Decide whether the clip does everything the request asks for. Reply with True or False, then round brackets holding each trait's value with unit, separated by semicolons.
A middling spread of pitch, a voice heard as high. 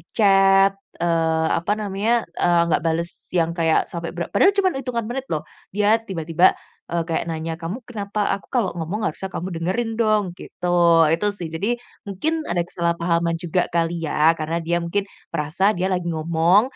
False (3.7 semitones; 175 Hz)